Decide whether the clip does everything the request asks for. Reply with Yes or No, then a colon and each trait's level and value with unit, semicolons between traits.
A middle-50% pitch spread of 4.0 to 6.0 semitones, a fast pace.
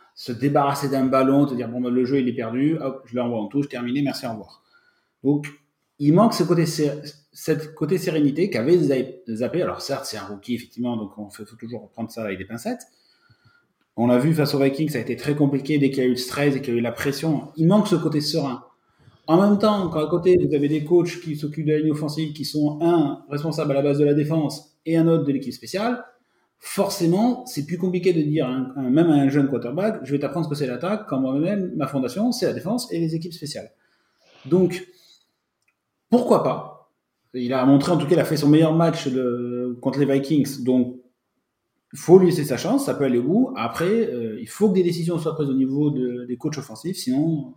Yes: average, 4.4 semitones; fast, 235 wpm